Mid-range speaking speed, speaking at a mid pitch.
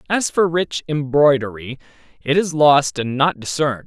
Yes: average, 155 wpm; medium, 145 Hz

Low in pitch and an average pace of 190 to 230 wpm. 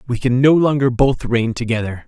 Yes: low, 125 Hz; fast, 205 wpm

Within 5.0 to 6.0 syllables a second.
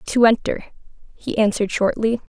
Yes: 5.6 syllables/s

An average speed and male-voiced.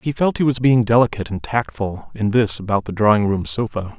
No: fast, 225 wpm; male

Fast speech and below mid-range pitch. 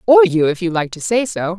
No: fast, 300 wpm; high, 195 Hz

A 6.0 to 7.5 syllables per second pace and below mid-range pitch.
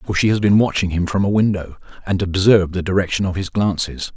Yes: 6.1 syllables/s; very low, 95 Hz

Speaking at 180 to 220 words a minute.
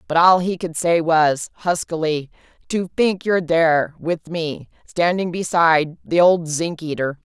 No: average, 140 wpm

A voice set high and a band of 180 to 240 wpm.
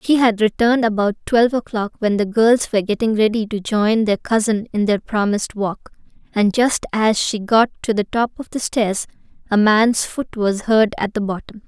Yes: high, 215 Hz; average, 200 wpm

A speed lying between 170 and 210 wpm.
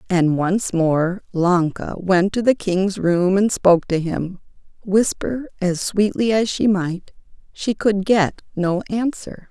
No: average, 150 wpm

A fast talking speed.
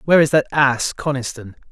No: average, 175 wpm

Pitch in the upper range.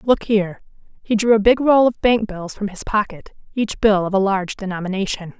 Yes: high, 205 Hz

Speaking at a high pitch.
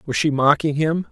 No: medium, 150 Hz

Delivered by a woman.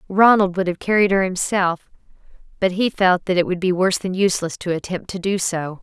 Yes: female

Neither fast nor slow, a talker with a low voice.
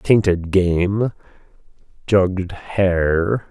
No: slow, 70 wpm; very low, 95 Hz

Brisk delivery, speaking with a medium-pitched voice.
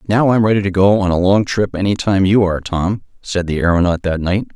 No: fast, 250 wpm; very low, 95 Hz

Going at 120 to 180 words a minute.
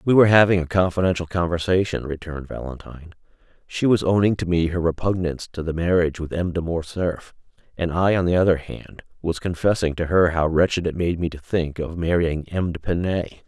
No: average, 190 wpm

